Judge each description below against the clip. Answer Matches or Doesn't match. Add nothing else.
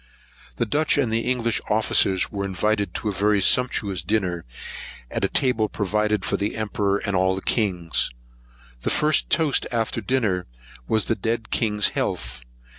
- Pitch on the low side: Matches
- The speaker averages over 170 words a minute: Doesn't match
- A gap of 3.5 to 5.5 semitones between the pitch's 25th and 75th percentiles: Doesn't match